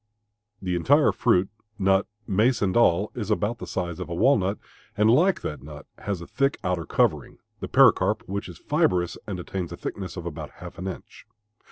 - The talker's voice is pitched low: Yes, very low, 95 Hz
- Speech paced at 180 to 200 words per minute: Yes, average, 190 wpm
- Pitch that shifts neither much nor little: Yes, average, 3.5 semitones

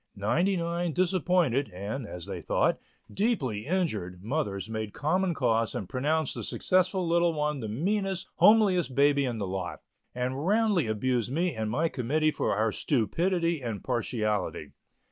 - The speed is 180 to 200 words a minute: No, average, 150 wpm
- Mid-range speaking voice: Yes, medium, 145 Hz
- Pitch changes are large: Yes, wide, 7.8 semitones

